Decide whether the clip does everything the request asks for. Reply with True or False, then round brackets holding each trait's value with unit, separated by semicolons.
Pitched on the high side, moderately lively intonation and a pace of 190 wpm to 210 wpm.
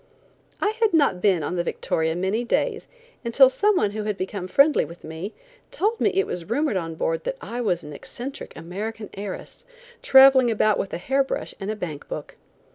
False (215 Hz; 7.2 semitones; 200 wpm)